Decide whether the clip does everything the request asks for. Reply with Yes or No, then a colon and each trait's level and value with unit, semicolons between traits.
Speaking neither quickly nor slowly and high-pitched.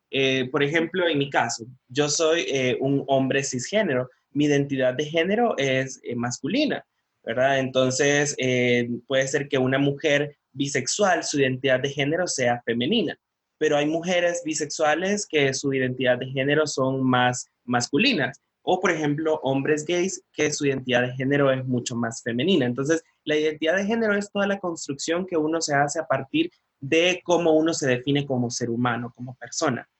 No: average, 170 wpm; medium, 140 Hz